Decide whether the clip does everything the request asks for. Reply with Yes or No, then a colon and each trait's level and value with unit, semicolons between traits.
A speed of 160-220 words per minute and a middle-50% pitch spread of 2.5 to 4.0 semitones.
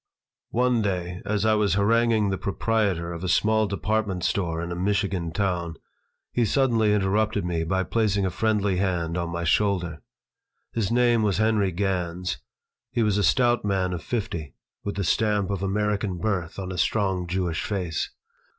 Yes: average, 170 wpm; average, 3.3 semitones